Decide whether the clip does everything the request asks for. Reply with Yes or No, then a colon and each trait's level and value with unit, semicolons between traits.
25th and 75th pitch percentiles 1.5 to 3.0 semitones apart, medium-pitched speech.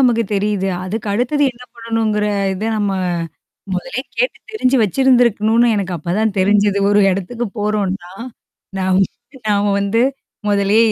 No: average, 2.7 semitones; high, 210 Hz